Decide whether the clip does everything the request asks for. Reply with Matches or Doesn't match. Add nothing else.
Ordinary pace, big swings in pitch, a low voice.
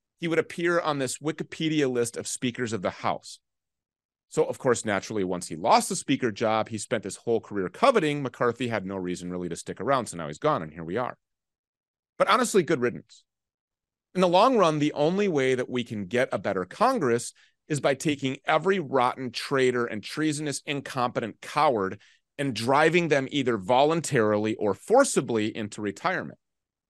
Matches